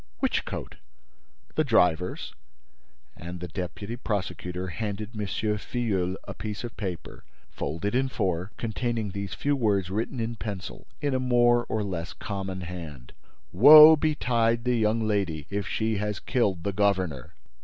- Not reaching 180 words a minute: Yes, average, 145 wpm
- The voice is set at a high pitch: No, low, 105 Hz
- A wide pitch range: No, average, 4.3 semitones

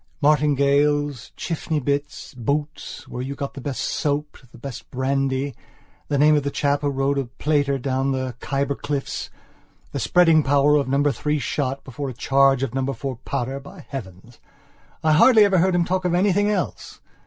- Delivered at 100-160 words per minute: No, average, 175 wpm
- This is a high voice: No, medium, 140 Hz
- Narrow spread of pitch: Yes, narrow, 1.9 semitones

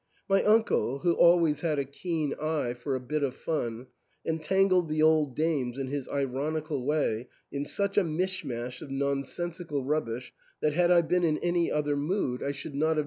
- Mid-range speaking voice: Yes, medium, 150 Hz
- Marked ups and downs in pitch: No, average, 3.7 semitones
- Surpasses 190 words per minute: Yes, average, 200 wpm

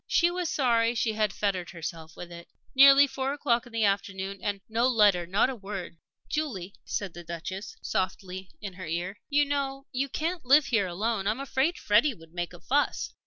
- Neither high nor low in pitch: No, high, 210 Hz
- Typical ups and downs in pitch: No, wide, 6.3 semitones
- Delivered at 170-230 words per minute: Yes, average, 200 wpm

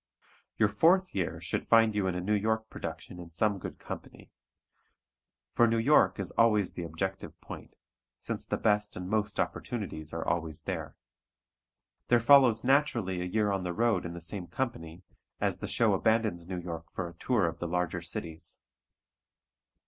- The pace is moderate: Yes, average, 170 wpm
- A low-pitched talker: Yes, very low, 95 Hz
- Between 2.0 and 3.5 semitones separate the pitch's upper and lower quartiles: No, average, 4.5 semitones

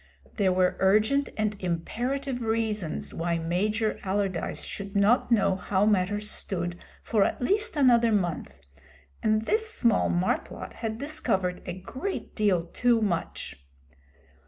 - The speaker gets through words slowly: Yes, slow, 130 wpm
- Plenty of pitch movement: No, average, 4.2 semitones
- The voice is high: Yes, high, 210 Hz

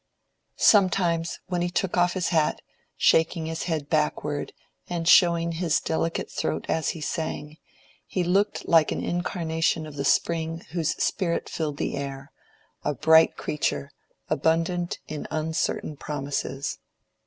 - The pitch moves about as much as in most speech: No, narrow, 2.3 semitones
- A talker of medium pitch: Yes, medium, 160 Hz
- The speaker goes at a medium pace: No, slow, 130 wpm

